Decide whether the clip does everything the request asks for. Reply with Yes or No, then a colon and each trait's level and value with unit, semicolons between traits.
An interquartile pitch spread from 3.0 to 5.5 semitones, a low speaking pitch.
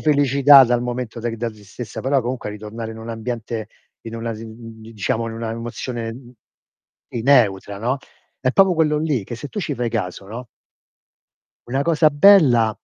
Yes: average, 3.3 semitones; low, 120 Hz